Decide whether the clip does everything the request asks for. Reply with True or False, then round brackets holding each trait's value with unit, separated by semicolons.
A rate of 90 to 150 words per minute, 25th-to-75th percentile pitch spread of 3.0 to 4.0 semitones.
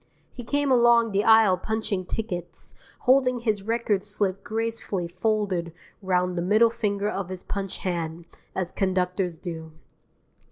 True (135 wpm; 3.7 semitones)